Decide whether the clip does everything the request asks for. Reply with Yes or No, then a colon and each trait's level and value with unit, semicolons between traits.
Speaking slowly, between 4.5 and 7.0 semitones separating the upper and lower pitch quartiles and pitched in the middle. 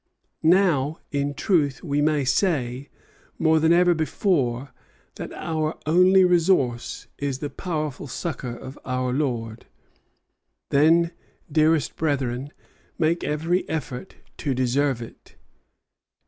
No: slow, 115 wpm; average, 3.9 semitones; medium, 150 Hz